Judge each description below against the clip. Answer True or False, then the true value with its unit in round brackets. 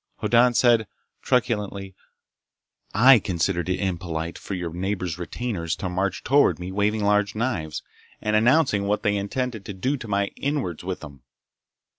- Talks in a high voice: False (100 Hz)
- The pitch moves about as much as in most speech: True (4.5 semitones)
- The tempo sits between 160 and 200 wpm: False (150 wpm)